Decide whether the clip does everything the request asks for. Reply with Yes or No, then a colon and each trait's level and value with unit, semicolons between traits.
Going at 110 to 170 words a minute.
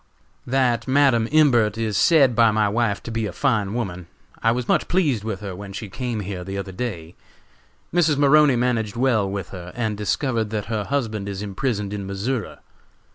No: average, 185 wpm